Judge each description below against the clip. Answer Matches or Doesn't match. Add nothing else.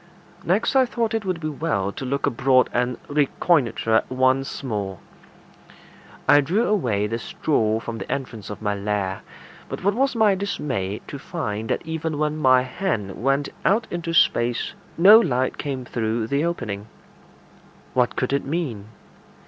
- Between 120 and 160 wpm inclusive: Matches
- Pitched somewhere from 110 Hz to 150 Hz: Matches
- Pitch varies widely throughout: Matches